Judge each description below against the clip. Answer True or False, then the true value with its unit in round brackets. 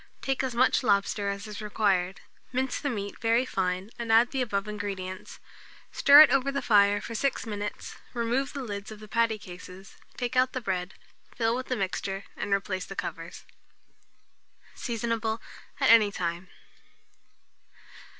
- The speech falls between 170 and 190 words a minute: False (160 wpm)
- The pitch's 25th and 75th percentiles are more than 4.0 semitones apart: False (3.5 semitones)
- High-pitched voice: True (215 Hz)